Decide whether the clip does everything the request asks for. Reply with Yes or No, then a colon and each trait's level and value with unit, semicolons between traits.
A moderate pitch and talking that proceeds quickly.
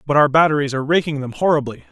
Yes: medium, 145 Hz; fast, 220 wpm